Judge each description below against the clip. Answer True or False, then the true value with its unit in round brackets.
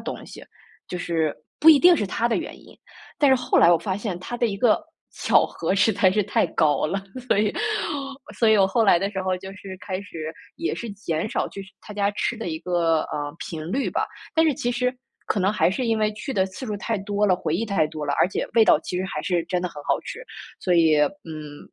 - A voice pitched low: False (195 Hz)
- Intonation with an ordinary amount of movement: True (4.5 semitones)